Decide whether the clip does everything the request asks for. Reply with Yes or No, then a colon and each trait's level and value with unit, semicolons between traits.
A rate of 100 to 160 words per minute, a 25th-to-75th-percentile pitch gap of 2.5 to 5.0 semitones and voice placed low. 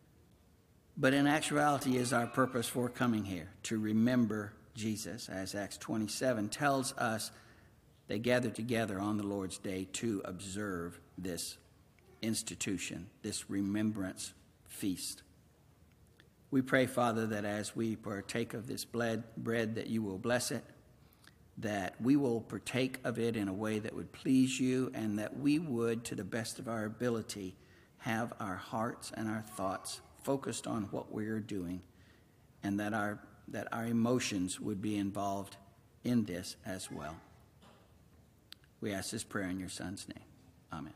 Yes: average, 150 wpm; average, 3.2 semitones; low, 110 Hz